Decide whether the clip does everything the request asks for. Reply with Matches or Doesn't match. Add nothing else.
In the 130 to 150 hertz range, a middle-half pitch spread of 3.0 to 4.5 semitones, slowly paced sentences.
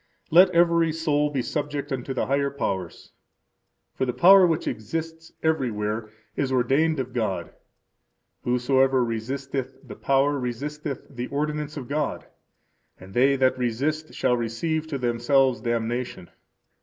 Matches